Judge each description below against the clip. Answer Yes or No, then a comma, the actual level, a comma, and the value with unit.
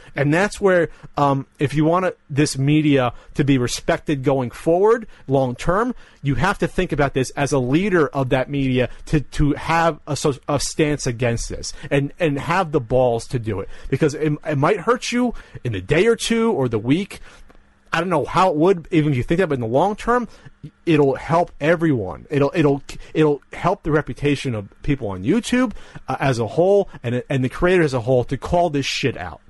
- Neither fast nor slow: No, fast, 210 wpm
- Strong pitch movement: No, average, 4.1 semitones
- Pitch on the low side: No, medium, 145 Hz